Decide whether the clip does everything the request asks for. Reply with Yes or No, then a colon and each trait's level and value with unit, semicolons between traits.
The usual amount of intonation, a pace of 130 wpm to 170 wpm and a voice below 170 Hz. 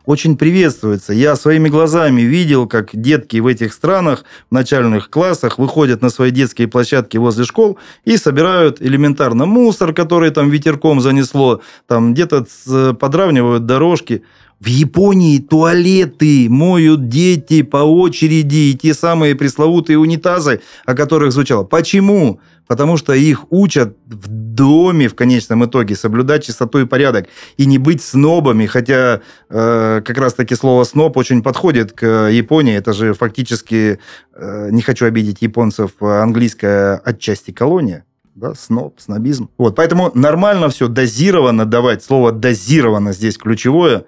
Yes: average, 5.0 semitones; average, 135 wpm; low, 135 Hz